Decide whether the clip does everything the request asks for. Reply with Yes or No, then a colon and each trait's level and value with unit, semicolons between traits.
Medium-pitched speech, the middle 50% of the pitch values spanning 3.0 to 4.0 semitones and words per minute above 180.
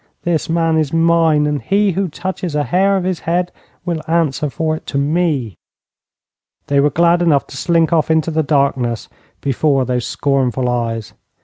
No: medium, 155 Hz; average, 3.5 semitones; average, 175 wpm